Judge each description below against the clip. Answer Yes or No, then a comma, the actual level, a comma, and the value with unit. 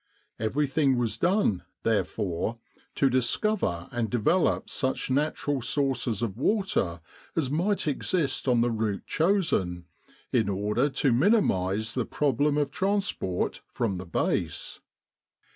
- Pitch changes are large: Yes, wide, 6.0 semitones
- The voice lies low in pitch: Yes, low, 125 Hz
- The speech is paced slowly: Yes, slow, 125 wpm